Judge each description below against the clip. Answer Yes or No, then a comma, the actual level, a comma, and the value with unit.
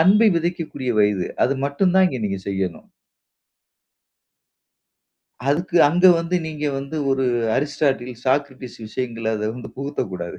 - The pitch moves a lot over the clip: Yes, wide, 6.1 semitones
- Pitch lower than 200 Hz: Yes, low, 135 Hz